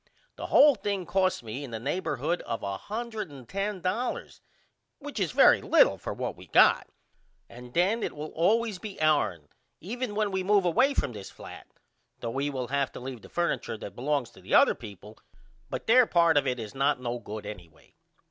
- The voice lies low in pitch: No, medium, 150 Hz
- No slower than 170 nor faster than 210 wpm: Yes, average, 185 wpm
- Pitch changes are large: Yes, wide, 8.9 semitones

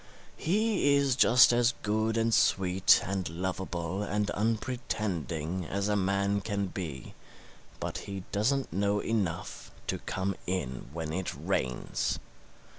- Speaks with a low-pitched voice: Yes, low, 100 Hz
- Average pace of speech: No, slow, 125 wpm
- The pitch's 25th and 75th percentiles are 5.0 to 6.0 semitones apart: No, average, 3.6 semitones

